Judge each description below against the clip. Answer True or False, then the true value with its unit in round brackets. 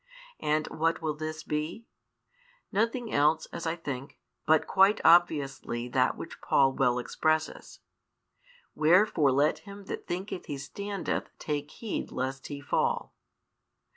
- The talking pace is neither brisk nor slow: False (130 wpm)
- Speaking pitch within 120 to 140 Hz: False (155 Hz)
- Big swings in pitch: False (4.2 semitones)